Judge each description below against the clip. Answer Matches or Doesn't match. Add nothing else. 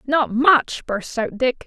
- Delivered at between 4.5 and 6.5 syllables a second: Doesn't match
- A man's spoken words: Doesn't match